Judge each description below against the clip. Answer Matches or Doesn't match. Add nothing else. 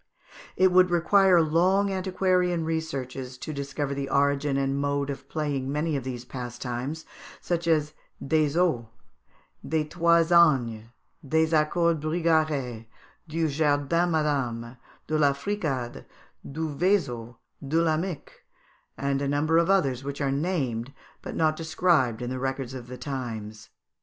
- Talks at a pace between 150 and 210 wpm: Doesn't match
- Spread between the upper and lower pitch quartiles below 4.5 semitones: Matches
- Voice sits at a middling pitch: Matches